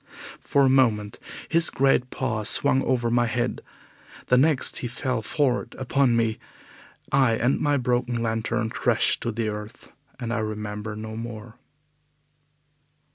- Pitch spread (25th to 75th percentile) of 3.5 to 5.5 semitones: No, average, 2.8 semitones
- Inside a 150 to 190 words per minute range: No, average, 140 wpm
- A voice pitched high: No, low, 120 Hz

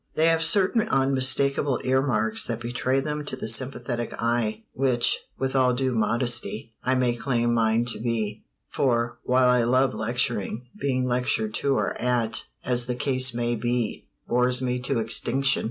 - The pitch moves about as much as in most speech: No, narrow, 2.0 semitones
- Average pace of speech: Yes, average, 160 wpm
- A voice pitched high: No, low, 125 Hz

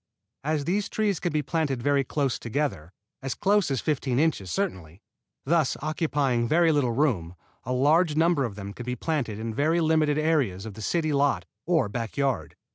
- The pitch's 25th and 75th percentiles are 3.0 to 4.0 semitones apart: No, average, 5.1 semitones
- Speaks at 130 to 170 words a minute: No, average, 180 wpm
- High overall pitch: No, medium, 145 Hz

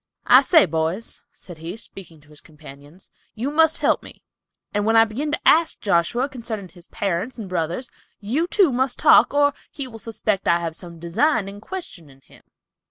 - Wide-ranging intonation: Yes, wide, 7.2 semitones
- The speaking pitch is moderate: No, high, 205 Hz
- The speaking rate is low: No, average, 185 wpm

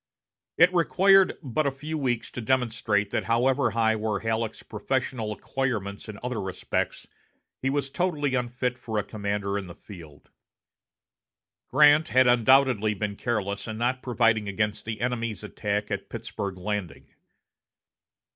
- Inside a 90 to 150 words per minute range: Yes, average, 140 wpm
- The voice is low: Yes, low, 115 Hz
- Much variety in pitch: No, average, 4.0 semitones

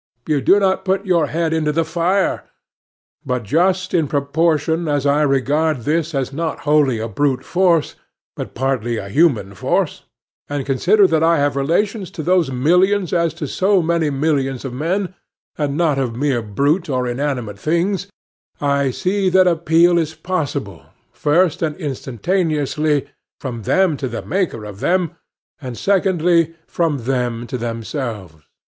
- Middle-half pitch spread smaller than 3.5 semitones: No, average, 4.5 semitones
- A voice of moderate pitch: Yes, medium, 150 Hz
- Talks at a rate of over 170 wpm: No, average, 155 wpm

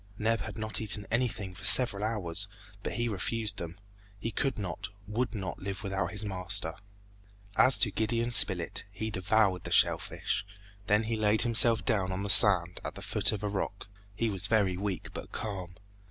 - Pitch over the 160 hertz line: No, low, 105 Hz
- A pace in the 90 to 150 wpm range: No, average, 185 wpm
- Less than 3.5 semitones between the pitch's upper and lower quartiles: Yes, average, 2.8 semitones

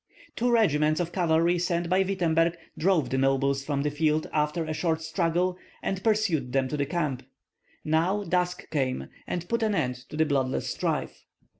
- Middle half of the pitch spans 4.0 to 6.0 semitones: No, average, 3.5 semitones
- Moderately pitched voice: Yes, medium, 160 Hz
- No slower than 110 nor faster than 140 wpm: No, average, 175 wpm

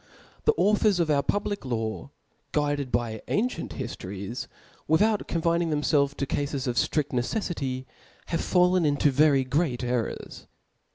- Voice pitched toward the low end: No, medium, 145 Hz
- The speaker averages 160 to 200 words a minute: No, average, 145 wpm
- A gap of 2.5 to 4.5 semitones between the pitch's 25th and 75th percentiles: No, average, 5.0 semitones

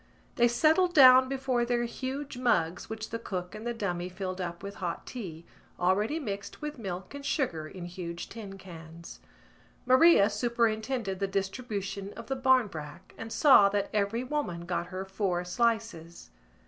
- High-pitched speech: Yes, high, 205 Hz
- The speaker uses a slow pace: No, average, 160 wpm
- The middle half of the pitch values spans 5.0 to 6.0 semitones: Yes, average, 5.3 semitones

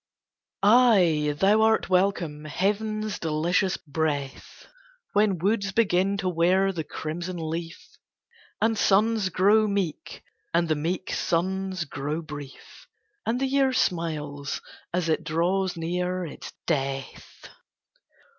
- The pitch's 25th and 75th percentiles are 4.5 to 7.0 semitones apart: No, average, 4.0 semitones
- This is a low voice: No, medium, 180 Hz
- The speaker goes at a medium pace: No, slow, 115 wpm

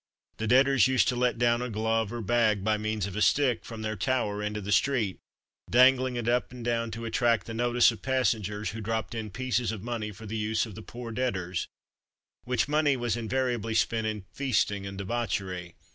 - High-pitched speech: No, low, 115 Hz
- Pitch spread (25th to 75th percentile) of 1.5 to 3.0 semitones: Yes, narrow, 2.5 semitones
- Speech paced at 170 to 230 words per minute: Yes, fast, 205 wpm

